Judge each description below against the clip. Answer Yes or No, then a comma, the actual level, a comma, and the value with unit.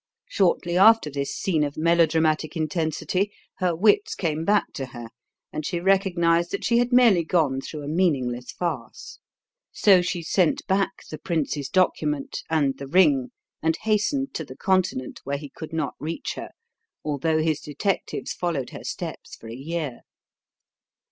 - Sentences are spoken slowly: No, average, 155 wpm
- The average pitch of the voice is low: No, medium, 160 Hz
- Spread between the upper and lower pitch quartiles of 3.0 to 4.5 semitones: Yes, average, 4.1 semitones